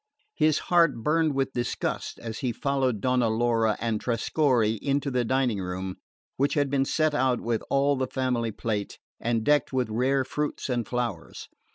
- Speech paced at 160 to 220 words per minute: Yes, average, 170 wpm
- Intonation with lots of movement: No, average, 3.3 semitones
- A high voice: No, low, 125 Hz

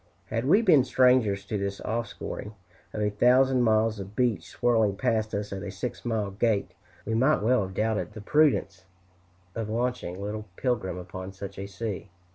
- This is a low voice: Yes, low, 110 Hz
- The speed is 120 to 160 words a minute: No, average, 175 wpm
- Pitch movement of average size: Yes, average, 3.7 semitones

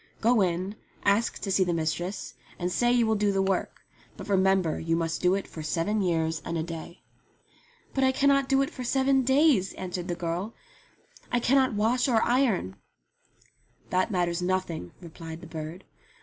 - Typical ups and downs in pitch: No, wide, 5.7 semitones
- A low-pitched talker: No, high, 190 Hz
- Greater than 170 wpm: Yes, average, 180 wpm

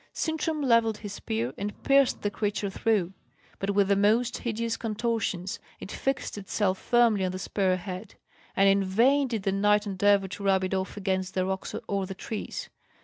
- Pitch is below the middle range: No, high, 205 Hz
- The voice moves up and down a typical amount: Yes, average, 3.0 semitones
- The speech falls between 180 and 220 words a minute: Yes, average, 185 wpm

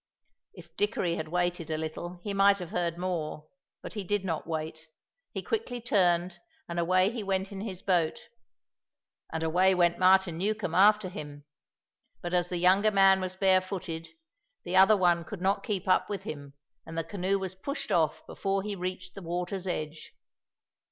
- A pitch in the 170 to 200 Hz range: Yes, medium, 185 Hz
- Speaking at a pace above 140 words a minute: Yes, average, 175 wpm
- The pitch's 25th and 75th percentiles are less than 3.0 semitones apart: Yes, narrow, 2.4 semitones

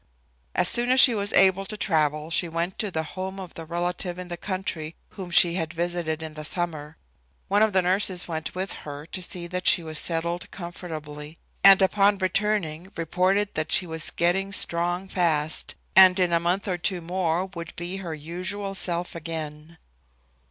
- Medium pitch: Yes, medium, 175 Hz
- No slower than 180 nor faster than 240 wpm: Yes, average, 185 wpm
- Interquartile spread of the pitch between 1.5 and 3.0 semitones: Yes, average, 2.7 semitones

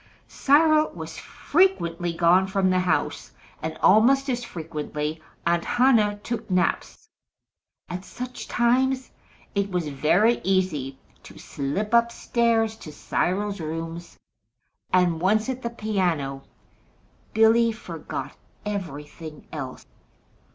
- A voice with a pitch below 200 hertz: Yes, high, 190 Hz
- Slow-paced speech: Yes, slow, 110 wpm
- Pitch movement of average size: No, wide, 6.1 semitones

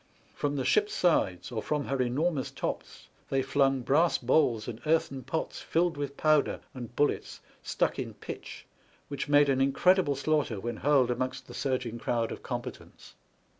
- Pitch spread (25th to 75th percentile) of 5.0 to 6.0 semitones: No, average, 3.2 semitones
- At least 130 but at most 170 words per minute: Yes, average, 165 wpm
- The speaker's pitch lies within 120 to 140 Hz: Yes, low, 135 Hz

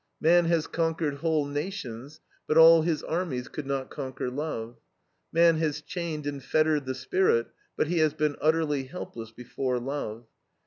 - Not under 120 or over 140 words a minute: No, average, 160 wpm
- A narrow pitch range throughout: No, average, 3.6 semitones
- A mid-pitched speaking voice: Yes, medium, 150 Hz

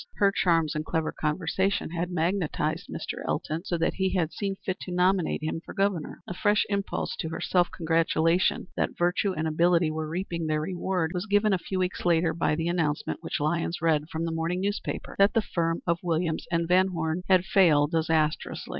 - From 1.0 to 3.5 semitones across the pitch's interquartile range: Yes, narrow, 2.5 semitones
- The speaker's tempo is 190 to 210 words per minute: Yes, average, 200 wpm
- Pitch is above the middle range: No, medium, 170 Hz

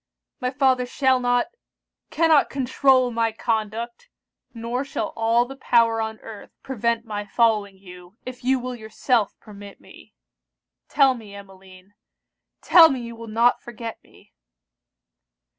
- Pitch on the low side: No, high, 235 Hz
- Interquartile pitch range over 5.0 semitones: No, average, 2.8 semitones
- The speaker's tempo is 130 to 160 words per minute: Yes, slow, 135 wpm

